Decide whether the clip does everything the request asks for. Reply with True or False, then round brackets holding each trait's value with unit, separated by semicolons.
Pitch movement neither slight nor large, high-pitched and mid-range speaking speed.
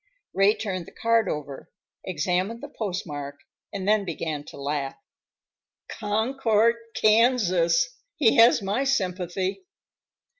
False (4.9 semitones; 200 Hz; 110 wpm)